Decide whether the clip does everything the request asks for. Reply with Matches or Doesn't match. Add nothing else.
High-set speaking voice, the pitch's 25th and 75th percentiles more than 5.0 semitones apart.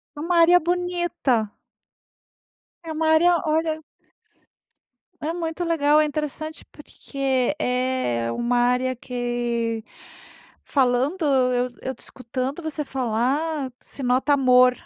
Doesn't match